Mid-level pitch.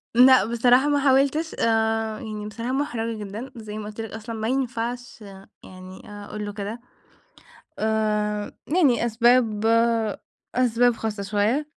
No: high, 225 Hz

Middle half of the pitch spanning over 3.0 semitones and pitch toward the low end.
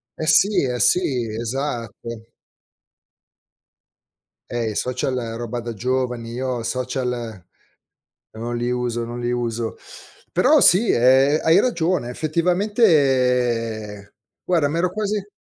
Yes: average, 4.9 semitones; low, 125 Hz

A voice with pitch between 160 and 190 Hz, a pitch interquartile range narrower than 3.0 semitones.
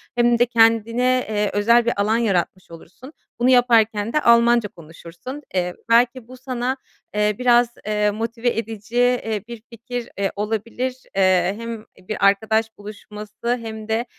No: high, 225 Hz; narrow, 2.5 semitones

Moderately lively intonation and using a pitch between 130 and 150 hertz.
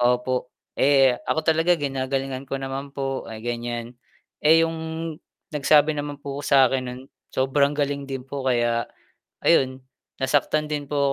No: narrow, 2.0 semitones; low, 135 Hz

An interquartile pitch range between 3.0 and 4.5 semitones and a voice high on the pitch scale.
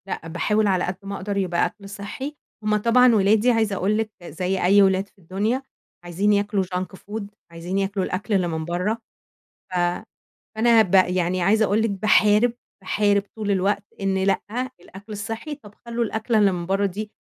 No: narrow, 2.4 semitones; high, 200 Hz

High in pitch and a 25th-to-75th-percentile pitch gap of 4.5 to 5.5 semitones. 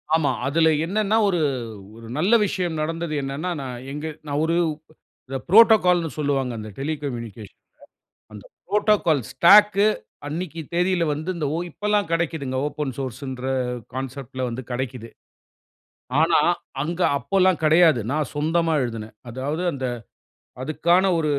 No: medium, 155 Hz; average, 4.8 semitones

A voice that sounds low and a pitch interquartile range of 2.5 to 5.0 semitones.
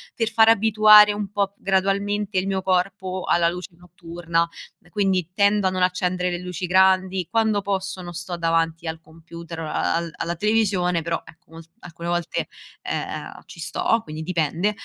No: medium, 185 Hz; average, 2.9 semitones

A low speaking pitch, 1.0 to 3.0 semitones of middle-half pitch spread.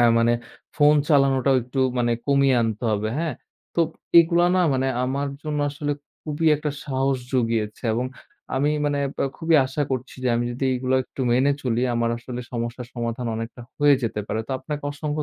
No: low, 130 Hz; average, 3.6 semitones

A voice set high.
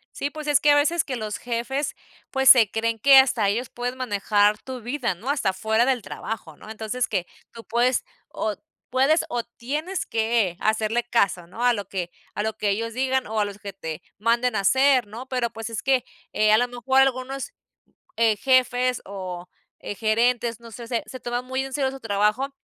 Yes: high, 235 Hz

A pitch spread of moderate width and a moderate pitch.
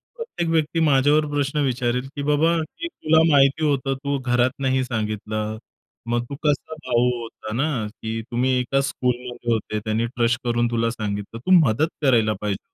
No: average, 3.9 semitones; low, 125 Hz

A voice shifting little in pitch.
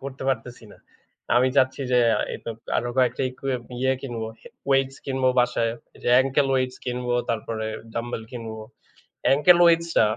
Yes: narrow, 2.3 semitones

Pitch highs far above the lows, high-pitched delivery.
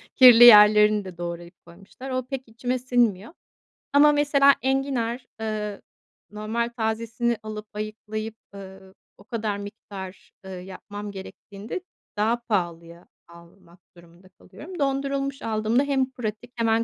No: average, 3.9 semitones; high, 220 Hz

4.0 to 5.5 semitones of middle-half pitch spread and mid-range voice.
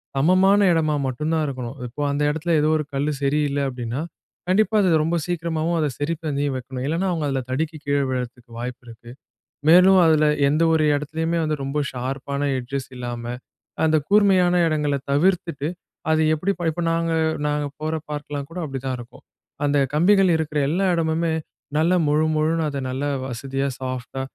No: average, 3.3 semitones; medium, 150 Hz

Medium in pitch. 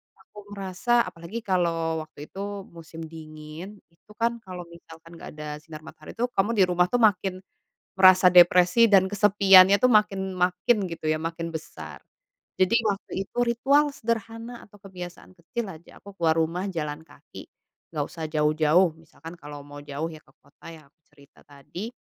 Yes: medium, 180 Hz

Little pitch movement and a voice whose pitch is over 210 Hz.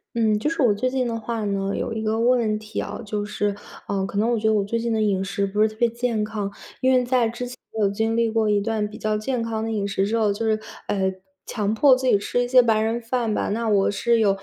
Yes: narrow, 2.2 semitones; high, 220 Hz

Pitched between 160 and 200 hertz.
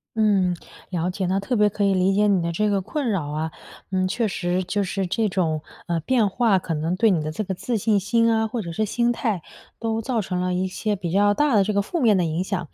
Yes: high, 195 Hz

